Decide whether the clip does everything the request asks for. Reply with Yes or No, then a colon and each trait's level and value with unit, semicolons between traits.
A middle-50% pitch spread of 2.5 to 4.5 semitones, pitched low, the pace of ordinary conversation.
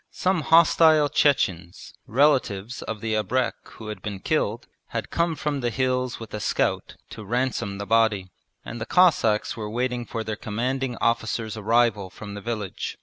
Yes: average, 3.7 semitones; low, 115 Hz; average, 165 wpm